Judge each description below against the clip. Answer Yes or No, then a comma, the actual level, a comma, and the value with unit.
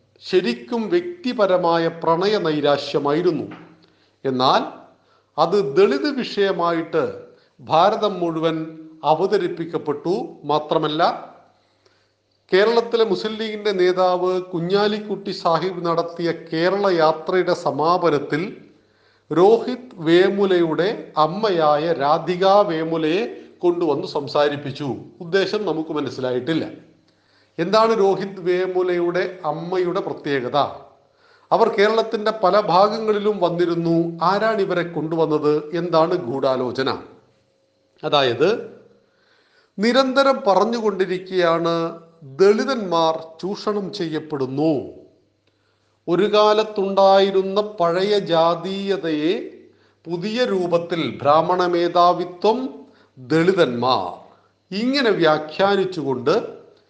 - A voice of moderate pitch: Yes, medium, 180 Hz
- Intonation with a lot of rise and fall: No, average, 4.6 semitones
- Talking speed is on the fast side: No, average, 65 wpm